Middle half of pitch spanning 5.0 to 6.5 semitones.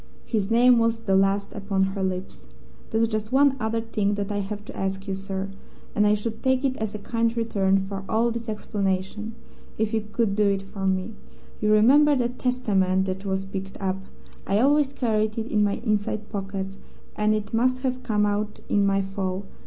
No: average, 2.7 semitones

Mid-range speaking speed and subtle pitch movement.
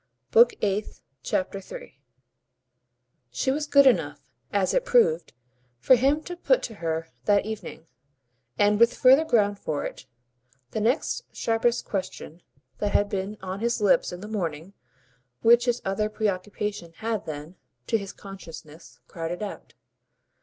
No: average, 145 wpm; average, 4.4 semitones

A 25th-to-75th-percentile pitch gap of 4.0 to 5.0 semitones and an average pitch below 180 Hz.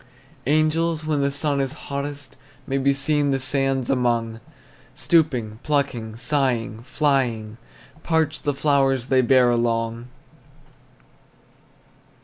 No: average, 3.3 semitones; low, 135 Hz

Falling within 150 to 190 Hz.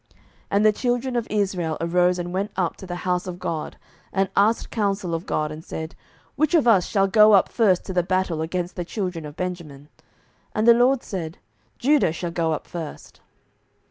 Yes: medium, 185 Hz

